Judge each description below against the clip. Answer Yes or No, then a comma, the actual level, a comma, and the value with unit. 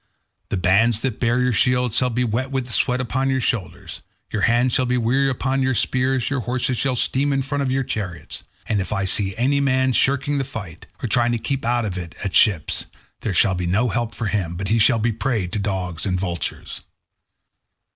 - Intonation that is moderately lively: Yes, average, 4.2 semitones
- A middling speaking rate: No, fast, 225 wpm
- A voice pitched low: Yes, low, 120 Hz